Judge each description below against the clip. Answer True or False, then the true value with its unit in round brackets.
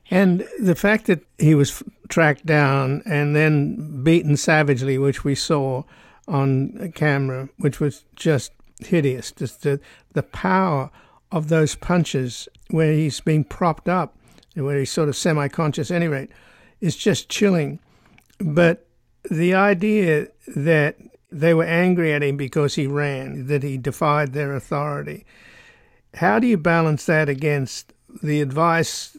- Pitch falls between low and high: True (155 Hz)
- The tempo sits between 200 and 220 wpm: False (145 wpm)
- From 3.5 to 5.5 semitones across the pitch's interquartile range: False (3.1 semitones)